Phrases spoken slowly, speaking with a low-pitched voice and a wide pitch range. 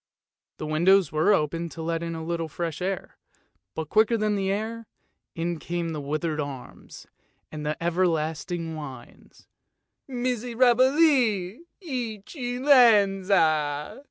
No: slow, 125 wpm; medium, 175 Hz; wide, 6.0 semitones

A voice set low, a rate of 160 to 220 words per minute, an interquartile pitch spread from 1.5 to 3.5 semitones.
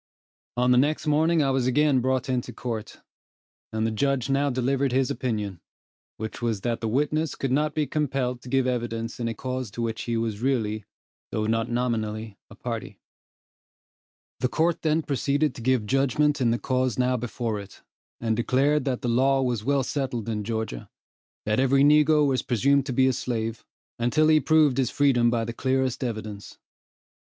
Yes: low, 125 Hz; average, 180 wpm; average, 3.2 semitones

